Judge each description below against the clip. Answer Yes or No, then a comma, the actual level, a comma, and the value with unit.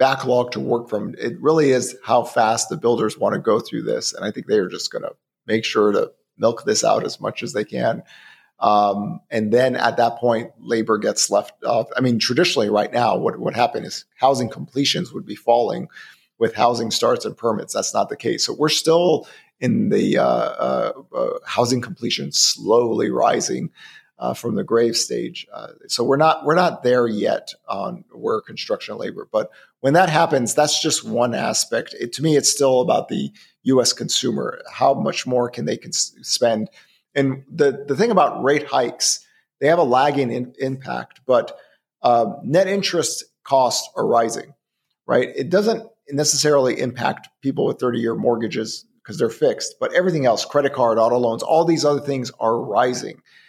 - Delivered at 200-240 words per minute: No, average, 185 wpm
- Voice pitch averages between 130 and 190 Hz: Yes, low, 135 Hz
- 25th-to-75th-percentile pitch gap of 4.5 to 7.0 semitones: Yes, wide, 5.5 semitones